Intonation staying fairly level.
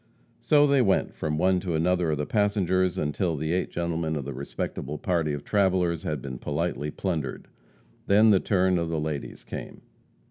No: average, 3.7 semitones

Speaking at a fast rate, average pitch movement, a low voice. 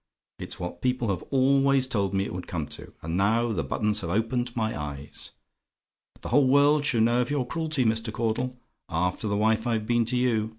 Yes: fast, 210 wpm; average, 4.2 semitones; low, 115 Hz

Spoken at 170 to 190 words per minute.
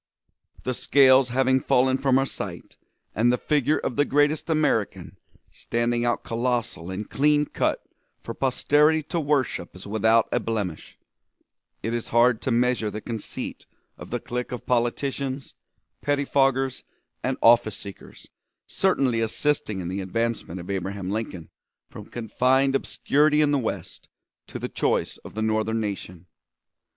No: average, 145 wpm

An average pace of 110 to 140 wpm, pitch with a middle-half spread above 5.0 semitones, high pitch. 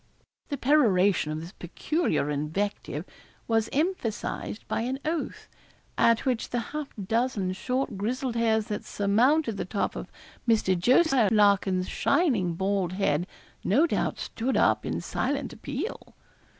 Yes: slow, 135 wpm; wide, 5.6 semitones; high, 225 Hz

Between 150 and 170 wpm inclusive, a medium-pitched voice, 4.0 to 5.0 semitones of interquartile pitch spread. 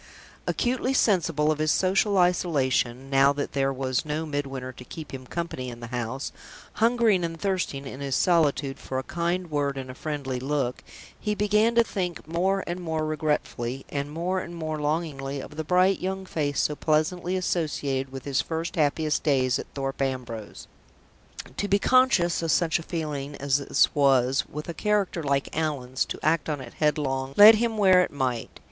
No: average, 185 wpm; medium, 150 Hz; average, 4.6 semitones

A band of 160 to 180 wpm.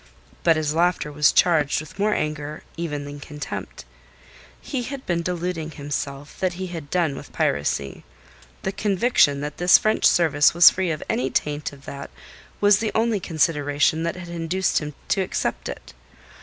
Yes: average, 170 wpm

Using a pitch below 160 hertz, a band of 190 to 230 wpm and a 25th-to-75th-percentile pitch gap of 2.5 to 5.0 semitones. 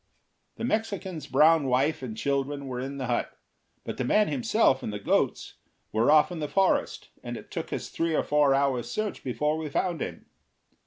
Yes: medium, 140 Hz; average, 195 wpm; average, 4.2 semitones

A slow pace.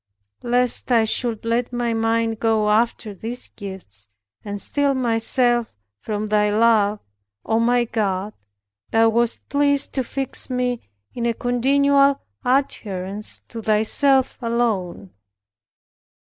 Yes: slow, 120 wpm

